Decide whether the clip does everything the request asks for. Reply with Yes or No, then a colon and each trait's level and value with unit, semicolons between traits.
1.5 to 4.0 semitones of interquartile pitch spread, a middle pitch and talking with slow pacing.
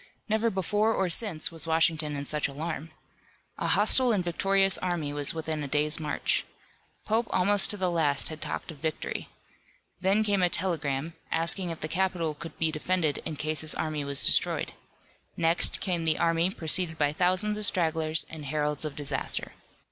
No: average, 3.3 semitones; medium, 165 Hz; average, 175 wpm